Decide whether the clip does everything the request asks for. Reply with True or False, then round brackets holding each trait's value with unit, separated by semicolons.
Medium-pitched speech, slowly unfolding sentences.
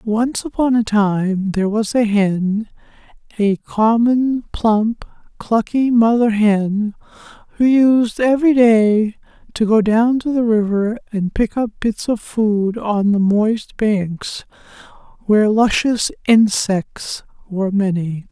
False (220 Hz; 130 wpm)